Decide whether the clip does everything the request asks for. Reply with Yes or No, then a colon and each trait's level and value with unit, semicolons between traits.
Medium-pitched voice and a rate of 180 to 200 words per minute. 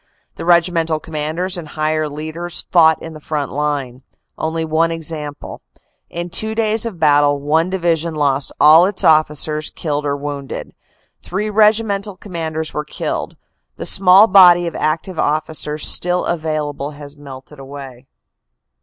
No: medium, 155 Hz; average, 145 wpm